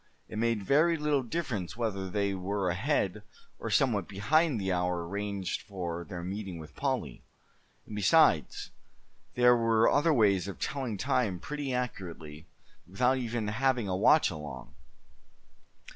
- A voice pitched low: Yes, low, 105 Hz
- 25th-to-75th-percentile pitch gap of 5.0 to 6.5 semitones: Yes, wide, 5.4 semitones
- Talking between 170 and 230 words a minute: No, average, 140 wpm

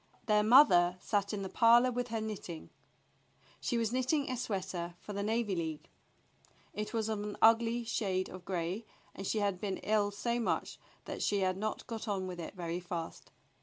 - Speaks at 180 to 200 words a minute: Yes, average, 190 wpm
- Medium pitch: No, high, 205 Hz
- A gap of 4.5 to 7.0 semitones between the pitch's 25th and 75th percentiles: No, average, 3.6 semitones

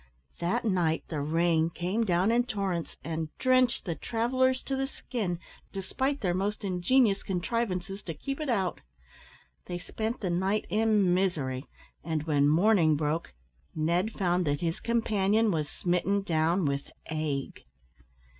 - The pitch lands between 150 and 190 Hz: Yes, medium, 185 Hz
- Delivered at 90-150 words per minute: Yes, average, 145 wpm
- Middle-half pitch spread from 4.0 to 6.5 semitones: Yes, average, 5.1 semitones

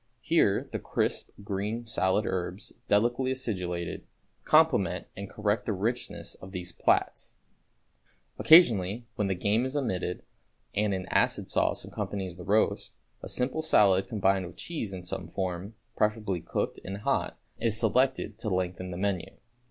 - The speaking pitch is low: Yes, low, 100 Hz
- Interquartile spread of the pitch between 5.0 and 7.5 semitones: No, average, 3.7 semitones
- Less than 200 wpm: Yes, average, 145 wpm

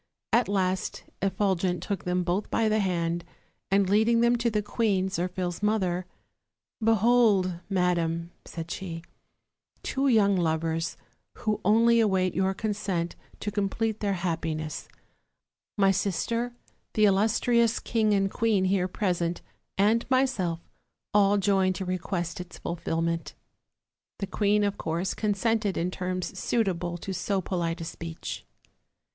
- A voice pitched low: No, high, 190 Hz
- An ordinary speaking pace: No, slow, 130 wpm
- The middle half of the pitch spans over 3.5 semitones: No, average, 3.2 semitones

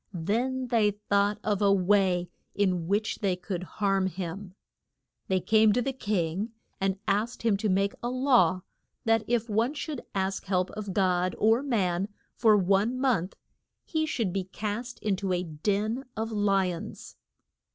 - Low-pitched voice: No, high, 205 Hz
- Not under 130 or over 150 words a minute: No, average, 160 wpm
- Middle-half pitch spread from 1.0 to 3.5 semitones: Yes, average, 3.1 semitones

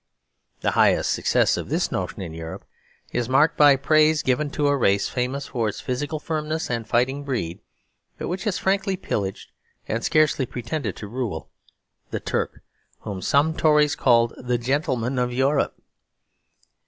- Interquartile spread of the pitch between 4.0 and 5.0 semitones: Yes, average, 4.3 semitones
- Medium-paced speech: Yes, average, 155 wpm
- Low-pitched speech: Yes, low, 130 Hz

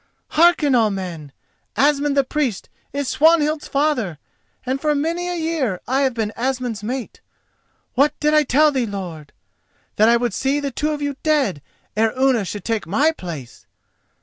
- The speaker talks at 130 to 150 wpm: No, average, 165 wpm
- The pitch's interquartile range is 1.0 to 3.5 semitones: No, wide, 5.6 semitones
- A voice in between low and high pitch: No, very high, 265 Hz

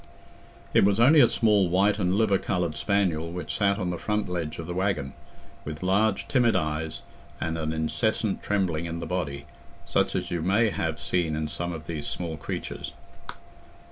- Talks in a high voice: No, very low, 90 Hz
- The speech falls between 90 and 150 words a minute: No, average, 180 wpm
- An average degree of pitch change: Yes, average, 4.0 semitones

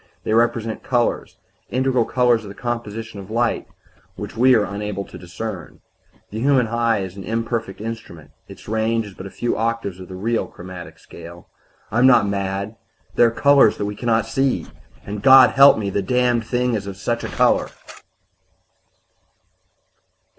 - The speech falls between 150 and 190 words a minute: Yes, average, 175 wpm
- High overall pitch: No, low, 115 Hz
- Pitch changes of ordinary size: Yes, average, 3.2 semitones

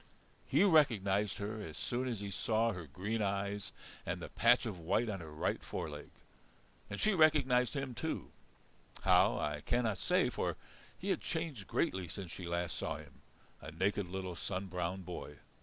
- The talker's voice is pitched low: Yes, low, 100 Hz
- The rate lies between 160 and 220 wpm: Yes, average, 175 wpm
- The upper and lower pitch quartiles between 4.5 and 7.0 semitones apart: Yes, average, 5.1 semitones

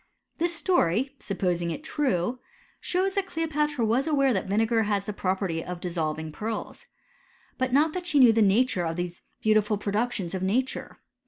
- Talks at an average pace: Yes, average, 170 wpm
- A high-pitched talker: Yes, high, 220 Hz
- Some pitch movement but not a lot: No, wide, 6.9 semitones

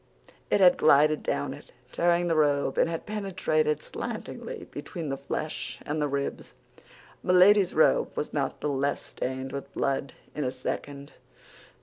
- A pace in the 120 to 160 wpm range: Yes, average, 150 wpm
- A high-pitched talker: No, medium, 150 Hz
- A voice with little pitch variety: No, average, 3.6 semitones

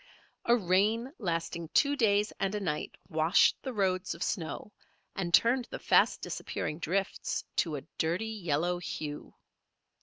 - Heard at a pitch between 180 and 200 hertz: Yes, medium, 185 Hz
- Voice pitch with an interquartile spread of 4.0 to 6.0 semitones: Yes, average, 4.3 semitones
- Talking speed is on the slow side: No, average, 145 wpm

